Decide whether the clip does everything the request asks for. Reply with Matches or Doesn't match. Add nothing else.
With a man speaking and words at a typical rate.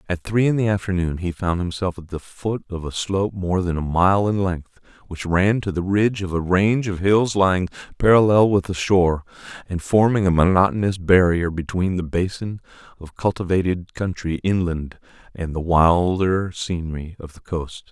Matches